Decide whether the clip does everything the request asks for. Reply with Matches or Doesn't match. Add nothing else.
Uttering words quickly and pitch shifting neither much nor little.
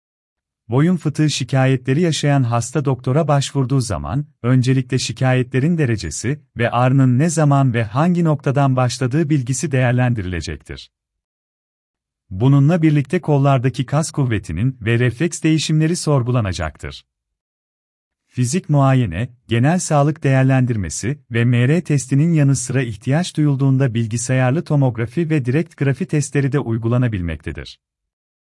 Doesn't match